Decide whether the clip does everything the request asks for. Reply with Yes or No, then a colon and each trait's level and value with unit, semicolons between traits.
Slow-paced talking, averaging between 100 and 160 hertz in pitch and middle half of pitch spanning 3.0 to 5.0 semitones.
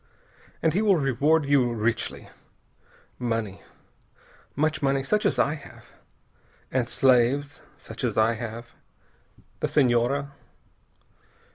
Yes: slow, 110 wpm; low, 135 Hz; average, 3.4 semitones